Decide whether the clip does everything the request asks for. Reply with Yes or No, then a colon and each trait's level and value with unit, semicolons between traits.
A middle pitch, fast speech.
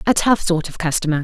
Yes: medium, 175 Hz; fast, 240 wpm